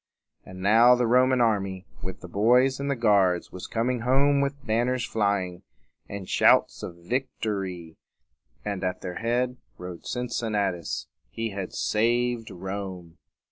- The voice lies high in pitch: No, low, 110 Hz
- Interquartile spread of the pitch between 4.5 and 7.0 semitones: Yes, average, 4.8 semitones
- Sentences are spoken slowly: No, average, 145 wpm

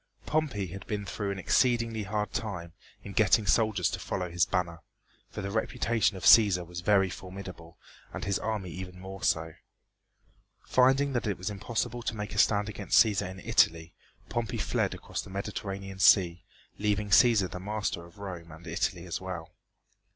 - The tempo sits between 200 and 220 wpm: No, average, 175 wpm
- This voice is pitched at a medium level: No, low, 100 Hz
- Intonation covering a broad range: No, average, 3.0 semitones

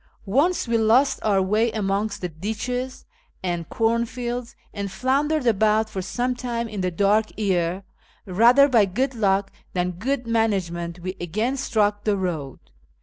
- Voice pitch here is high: Yes, high, 215 Hz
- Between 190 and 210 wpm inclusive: No, average, 145 wpm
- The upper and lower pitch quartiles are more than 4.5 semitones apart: No, average, 4.0 semitones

